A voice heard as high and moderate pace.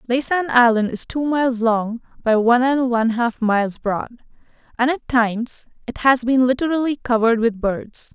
Yes: high, 245 Hz; average, 170 wpm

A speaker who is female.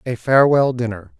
No: male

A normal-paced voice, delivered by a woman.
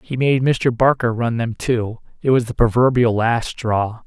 No: average, 175 wpm; male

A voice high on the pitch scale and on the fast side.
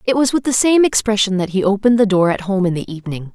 Yes: high, 205 Hz; fast, 285 wpm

